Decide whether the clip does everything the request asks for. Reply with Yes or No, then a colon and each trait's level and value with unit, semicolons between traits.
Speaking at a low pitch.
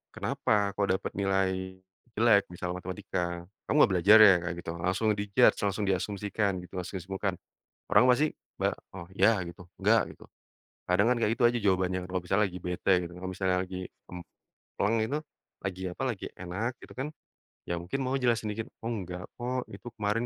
Yes: low, 100 Hz